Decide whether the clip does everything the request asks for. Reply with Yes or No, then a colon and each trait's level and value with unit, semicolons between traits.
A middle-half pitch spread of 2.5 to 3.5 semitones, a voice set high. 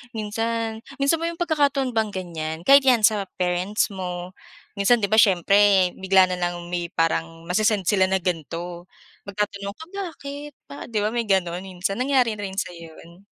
No: average, 4.3 semitones; high, 200 Hz